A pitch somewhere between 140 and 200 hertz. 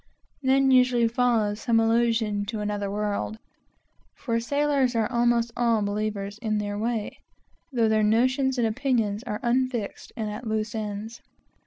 No: high, 225 Hz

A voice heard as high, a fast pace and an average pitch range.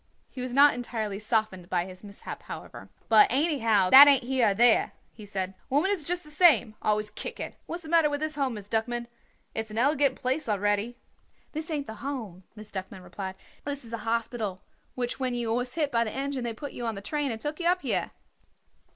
Yes: high, 240 Hz; fast, 220 wpm; average, 5.0 semitones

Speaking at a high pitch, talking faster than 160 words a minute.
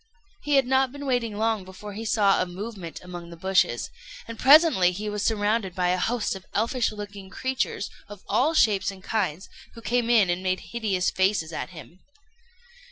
Yes: high, 205 Hz; average, 180 wpm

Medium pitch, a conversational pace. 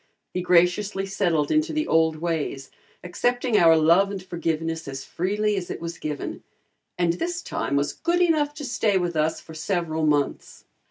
Yes: medium, 175 Hz; average, 170 wpm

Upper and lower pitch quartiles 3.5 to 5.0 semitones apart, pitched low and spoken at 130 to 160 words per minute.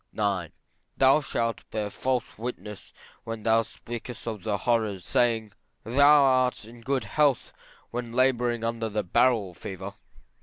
No: average, 2.9 semitones; low, 115 Hz; average, 140 wpm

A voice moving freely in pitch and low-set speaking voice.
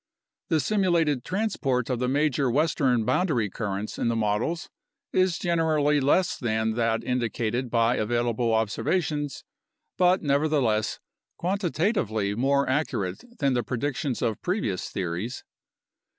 Yes: wide, 5.9 semitones; low, 130 Hz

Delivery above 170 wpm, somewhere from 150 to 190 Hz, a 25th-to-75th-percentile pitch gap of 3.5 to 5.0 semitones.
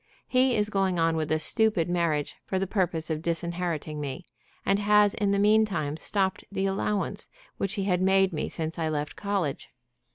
Yes: average, 190 wpm; medium, 185 Hz; average, 3.9 semitones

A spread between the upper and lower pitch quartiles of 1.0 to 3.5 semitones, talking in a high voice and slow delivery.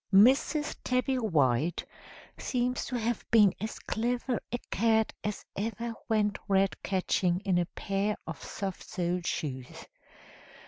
No: average, 4.4 semitones; high, 210 Hz; slow, 130 wpm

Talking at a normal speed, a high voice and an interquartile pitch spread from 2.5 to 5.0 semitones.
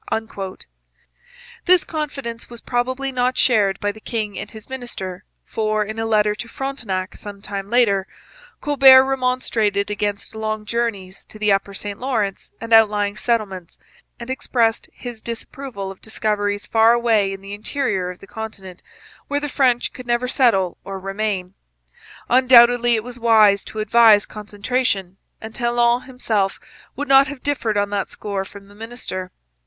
Yes: average, 155 wpm; high, 220 Hz; average, 3.3 semitones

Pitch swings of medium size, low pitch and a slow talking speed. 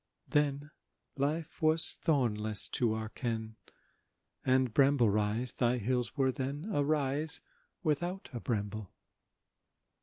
Yes: average, 4.7 semitones; low, 130 Hz; slow, 115 wpm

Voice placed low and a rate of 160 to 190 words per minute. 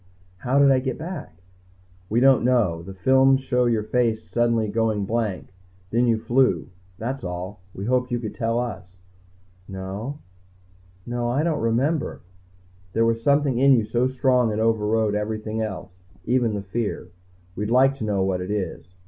Yes: low, 115 Hz; average, 170 wpm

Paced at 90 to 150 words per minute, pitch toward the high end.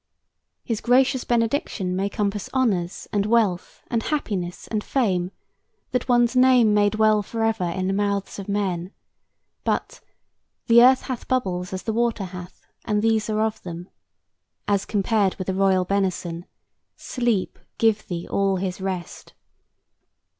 Yes: average, 145 wpm; high, 205 Hz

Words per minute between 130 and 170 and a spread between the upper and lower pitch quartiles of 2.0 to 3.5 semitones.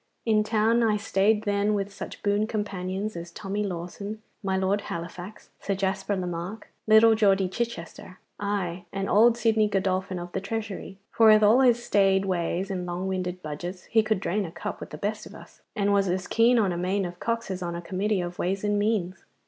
No: fast, 205 wpm; narrow, 2.6 semitones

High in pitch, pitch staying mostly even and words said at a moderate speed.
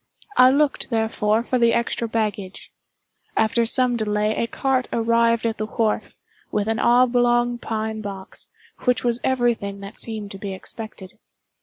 Yes: high, 230 Hz; narrow, 2.1 semitones; average, 155 wpm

